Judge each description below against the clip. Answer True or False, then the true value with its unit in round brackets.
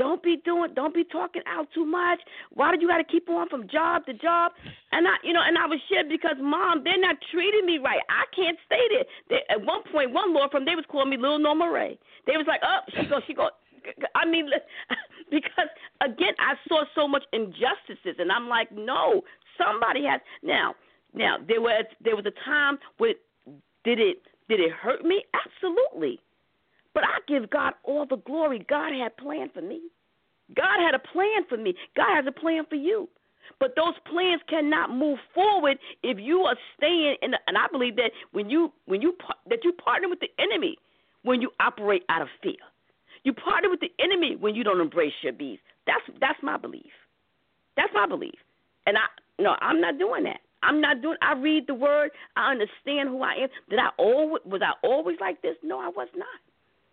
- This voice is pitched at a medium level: False (315 Hz)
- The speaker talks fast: True (210 wpm)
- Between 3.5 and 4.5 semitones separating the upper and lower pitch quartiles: True (4.1 semitones)